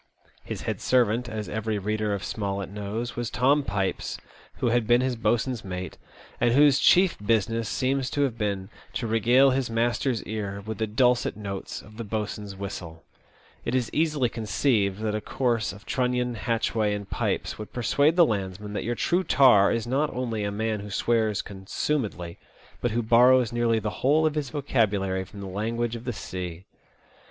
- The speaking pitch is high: No, low, 115 Hz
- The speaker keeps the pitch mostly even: No, average, 3.3 semitones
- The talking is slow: No, average, 180 wpm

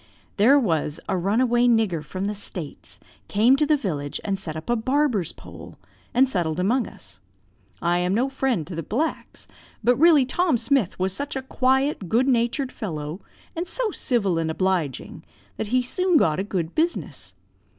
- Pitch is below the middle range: No, high, 220 Hz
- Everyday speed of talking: Yes, average, 170 wpm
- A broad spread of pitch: Yes, wide, 7.0 semitones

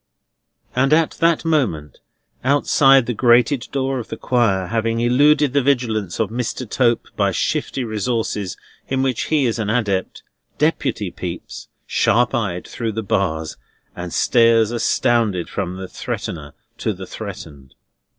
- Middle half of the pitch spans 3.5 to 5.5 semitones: Yes, average, 4.9 semitones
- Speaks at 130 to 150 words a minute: Yes, average, 140 wpm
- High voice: No, low, 115 Hz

